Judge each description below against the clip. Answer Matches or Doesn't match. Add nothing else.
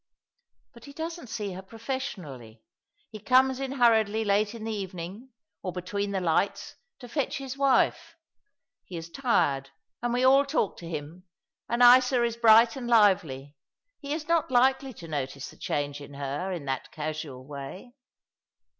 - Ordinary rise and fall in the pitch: Doesn't match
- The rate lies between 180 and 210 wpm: Doesn't match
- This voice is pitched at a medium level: Doesn't match